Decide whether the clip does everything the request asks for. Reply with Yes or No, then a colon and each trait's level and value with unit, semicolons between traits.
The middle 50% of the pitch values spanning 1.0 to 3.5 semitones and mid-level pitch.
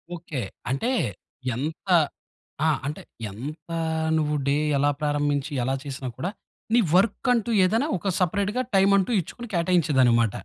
No: wide, 5.4 semitones; medium, 155 Hz